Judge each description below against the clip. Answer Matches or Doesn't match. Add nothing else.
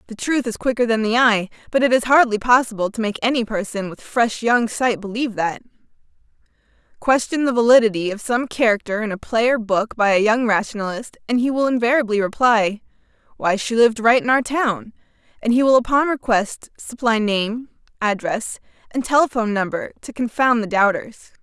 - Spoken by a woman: Matches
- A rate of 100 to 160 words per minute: Doesn't match